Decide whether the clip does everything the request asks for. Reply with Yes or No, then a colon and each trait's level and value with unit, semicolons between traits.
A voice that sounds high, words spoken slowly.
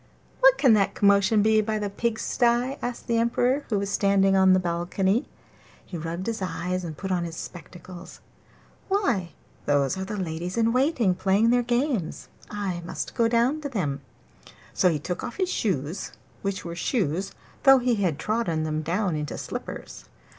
No: high, 195 Hz; average, 175 wpm